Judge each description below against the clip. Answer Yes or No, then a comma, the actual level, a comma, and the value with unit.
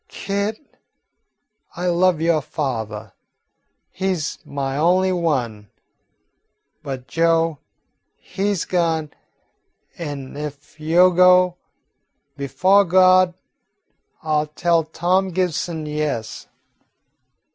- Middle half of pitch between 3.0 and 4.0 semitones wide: Yes, average, 3.7 semitones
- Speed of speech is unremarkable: No, slow, 90 wpm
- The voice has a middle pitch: Yes, medium, 165 Hz